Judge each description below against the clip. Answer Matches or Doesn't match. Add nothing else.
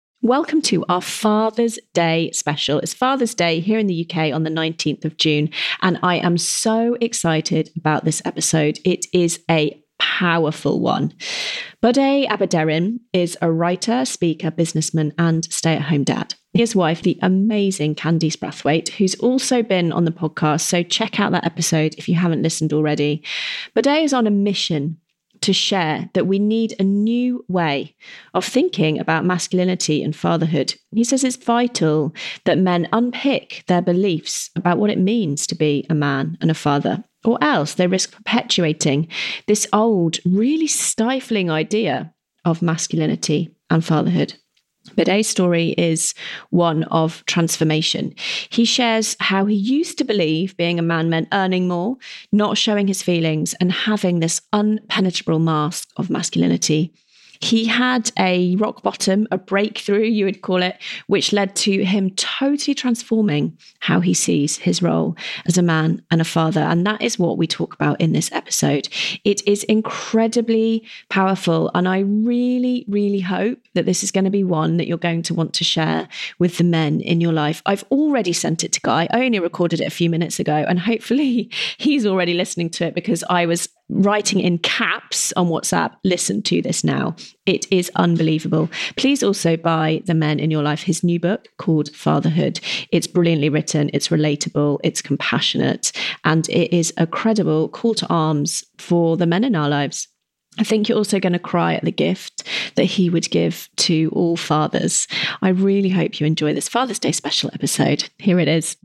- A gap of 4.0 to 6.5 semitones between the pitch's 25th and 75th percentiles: Matches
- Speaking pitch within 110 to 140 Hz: Doesn't match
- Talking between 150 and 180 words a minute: Matches